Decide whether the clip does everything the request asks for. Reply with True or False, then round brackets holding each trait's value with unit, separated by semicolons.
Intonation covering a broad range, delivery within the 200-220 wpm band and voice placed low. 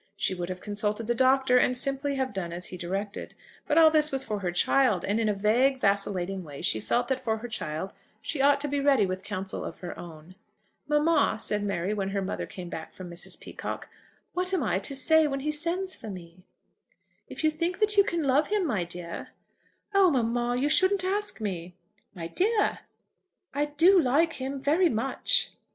False (7.7 semitones; 205 wpm; 245 Hz)